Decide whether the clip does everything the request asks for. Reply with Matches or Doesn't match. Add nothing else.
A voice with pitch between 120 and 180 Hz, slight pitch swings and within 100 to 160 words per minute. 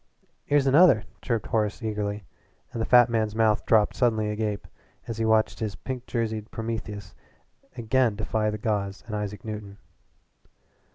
Doesn't match